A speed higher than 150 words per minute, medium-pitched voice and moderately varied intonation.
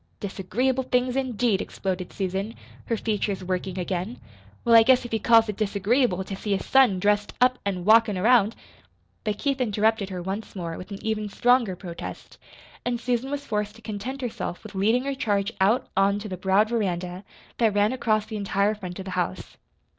No: average, 190 wpm; high, 210 Hz; average, 3.6 semitones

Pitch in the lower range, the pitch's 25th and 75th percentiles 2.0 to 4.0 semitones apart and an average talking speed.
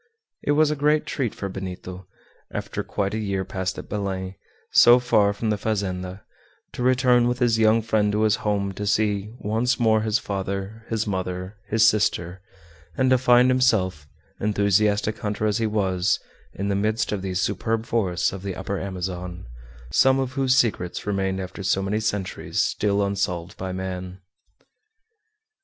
Yes: low, 105 Hz; average, 2.9 semitones; average, 165 wpm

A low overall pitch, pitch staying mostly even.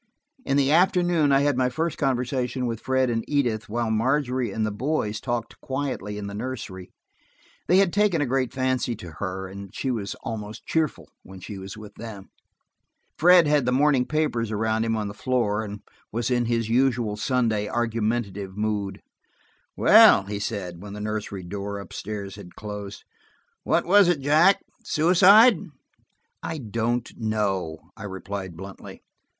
No: low, 115 Hz; average, 4.6 semitones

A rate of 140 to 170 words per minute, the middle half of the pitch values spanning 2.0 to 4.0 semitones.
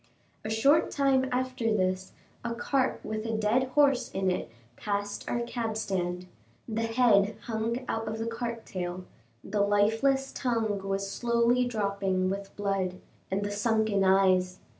Yes: average, 150 wpm; average, 3.3 semitones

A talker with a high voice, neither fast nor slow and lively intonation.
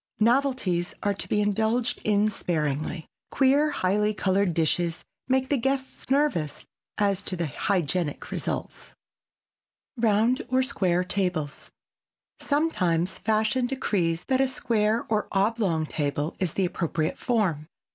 No: high, 205 Hz; slow, 125 wpm; wide, 5.9 semitones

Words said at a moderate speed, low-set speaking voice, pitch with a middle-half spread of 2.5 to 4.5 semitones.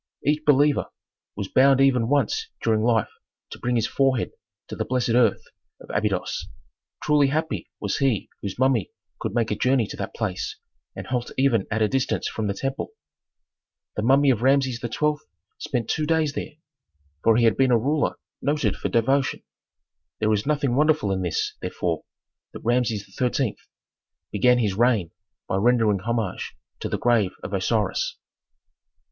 Yes: average, 165 wpm; low, 120 Hz; average, 4.1 semitones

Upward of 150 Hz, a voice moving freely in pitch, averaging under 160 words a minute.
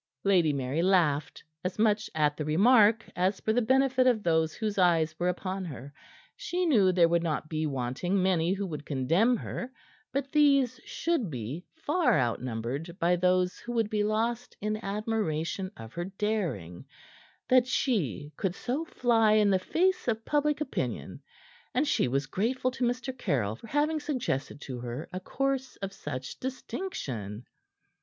No: high, 190 Hz; wide, 8.0 semitones; average, 165 wpm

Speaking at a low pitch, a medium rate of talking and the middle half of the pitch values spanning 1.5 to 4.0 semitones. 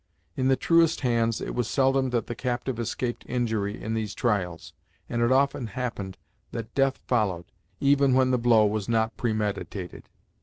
Yes: low, 120 Hz; average, 165 wpm; average, 3.2 semitones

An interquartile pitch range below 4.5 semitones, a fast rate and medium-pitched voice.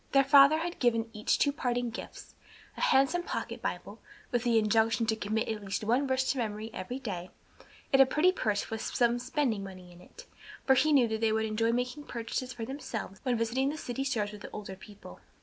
No: average, 3.7 semitones; fast, 210 wpm; high, 235 Hz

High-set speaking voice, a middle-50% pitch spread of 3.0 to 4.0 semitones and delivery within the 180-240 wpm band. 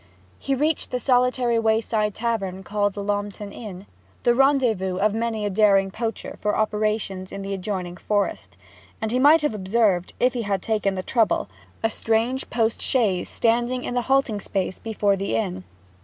No: high, 215 Hz; average, 3.3 semitones; average, 170 wpm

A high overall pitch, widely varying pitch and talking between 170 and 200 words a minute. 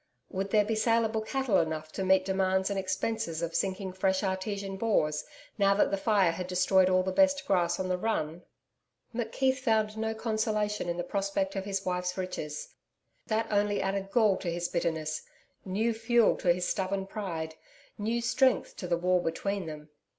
No: high, 195 Hz; average, 3.2 semitones; average, 180 wpm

